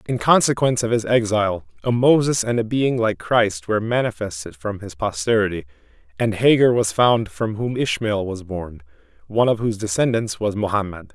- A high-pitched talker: No, low, 115 Hz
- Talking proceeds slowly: No, average, 170 wpm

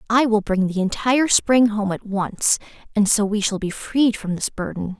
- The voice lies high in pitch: Yes, high, 210 Hz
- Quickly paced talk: Yes, fast, 215 wpm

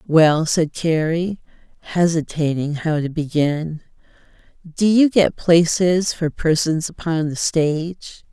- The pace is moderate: No, slow, 115 wpm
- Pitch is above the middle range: No, medium, 165 Hz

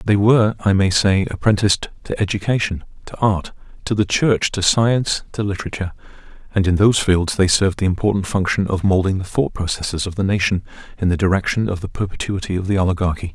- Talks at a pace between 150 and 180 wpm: No, average, 195 wpm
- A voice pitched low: Yes, very low, 95 Hz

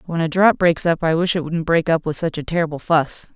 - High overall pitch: No, medium, 165 Hz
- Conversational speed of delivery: No, fast, 285 wpm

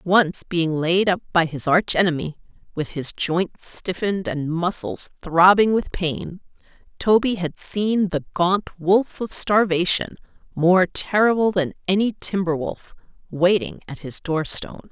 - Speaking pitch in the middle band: Yes, medium, 180 Hz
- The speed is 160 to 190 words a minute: No, average, 140 wpm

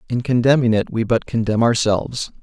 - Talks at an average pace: Yes, average, 175 wpm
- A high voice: No, low, 115 Hz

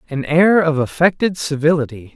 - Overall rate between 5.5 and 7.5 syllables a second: No, 5.1 syllables/s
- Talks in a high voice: No, medium, 155 Hz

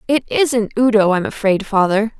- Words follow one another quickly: No, average, 165 wpm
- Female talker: Yes, female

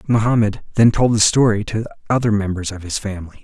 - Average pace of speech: Yes, average, 190 wpm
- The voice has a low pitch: Yes, low, 105 Hz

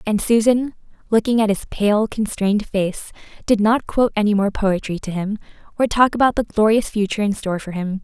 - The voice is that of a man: No, female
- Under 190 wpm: No, average, 195 wpm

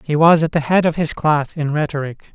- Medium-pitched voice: Yes, medium, 150 Hz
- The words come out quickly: Yes, fast, 255 wpm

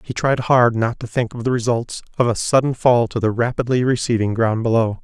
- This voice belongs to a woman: No, male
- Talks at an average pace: No, fast, 225 wpm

